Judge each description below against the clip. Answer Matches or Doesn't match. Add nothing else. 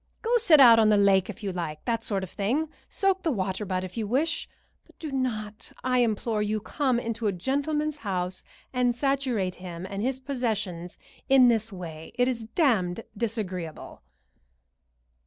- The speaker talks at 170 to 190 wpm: Matches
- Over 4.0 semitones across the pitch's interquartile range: Matches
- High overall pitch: Matches